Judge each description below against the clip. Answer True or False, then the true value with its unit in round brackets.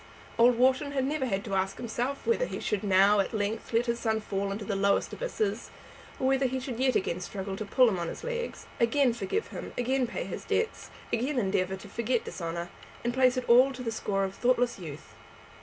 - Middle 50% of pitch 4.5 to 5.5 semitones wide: True (4.8 semitones)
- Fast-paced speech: True (220 wpm)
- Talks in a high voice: True (235 Hz)